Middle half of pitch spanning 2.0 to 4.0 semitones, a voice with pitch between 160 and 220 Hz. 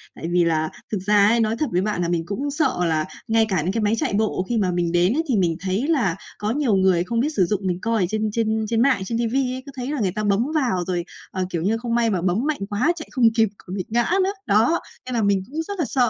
No: average, 4.7 semitones; high, 215 Hz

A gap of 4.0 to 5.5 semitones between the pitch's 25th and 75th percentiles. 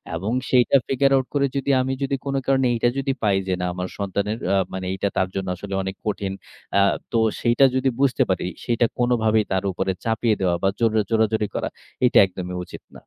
Yes: average, 4.9 semitones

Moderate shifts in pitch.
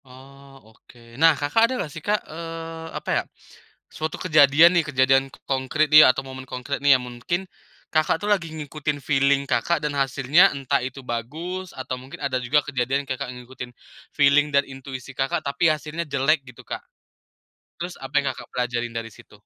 Yes: average, 3.0 semitones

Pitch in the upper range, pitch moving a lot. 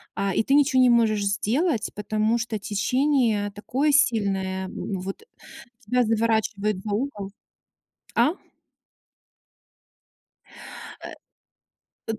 No: high, 220 Hz; average, 3.7 semitones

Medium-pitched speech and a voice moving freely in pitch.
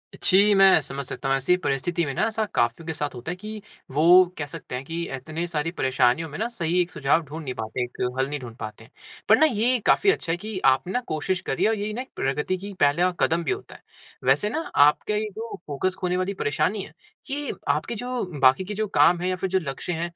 Yes: medium, 170 Hz; wide, 6.3 semitones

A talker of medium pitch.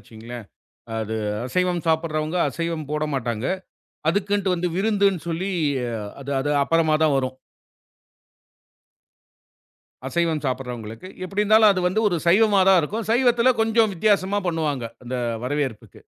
Yes: medium, 165 Hz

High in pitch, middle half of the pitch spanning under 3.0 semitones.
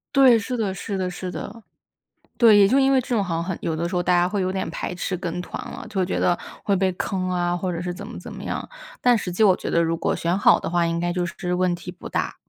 No: medium, 180 Hz; narrow, 2.5 semitones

